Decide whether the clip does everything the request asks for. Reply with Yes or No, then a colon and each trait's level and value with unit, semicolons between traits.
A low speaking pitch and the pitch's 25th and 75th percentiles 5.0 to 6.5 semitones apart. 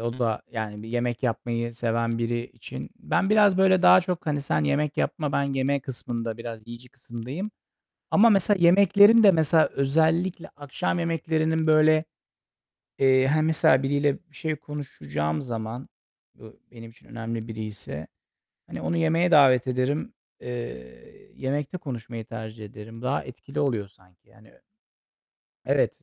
Yes: low, 130 Hz; wide, 5.6 semitones